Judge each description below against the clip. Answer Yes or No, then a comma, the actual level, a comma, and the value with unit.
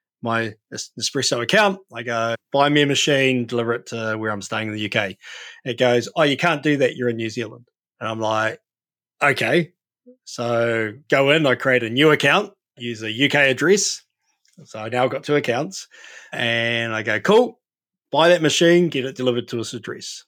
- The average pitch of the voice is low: Yes, low, 125 Hz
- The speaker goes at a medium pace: Yes, average, 190 wpm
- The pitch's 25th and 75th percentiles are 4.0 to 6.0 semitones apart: Yes, average, 4.3 semitones